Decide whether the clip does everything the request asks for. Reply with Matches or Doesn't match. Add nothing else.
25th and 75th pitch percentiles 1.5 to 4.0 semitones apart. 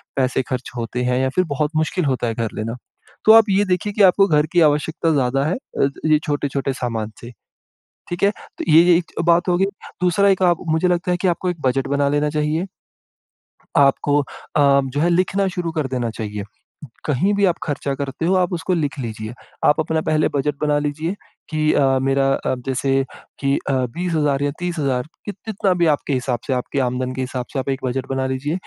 Doesn't match